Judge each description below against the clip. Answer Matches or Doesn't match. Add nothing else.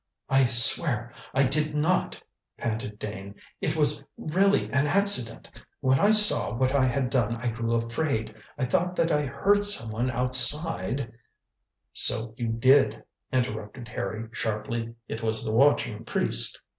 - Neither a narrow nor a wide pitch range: Matches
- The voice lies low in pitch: Matches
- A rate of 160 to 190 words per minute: Doesn't match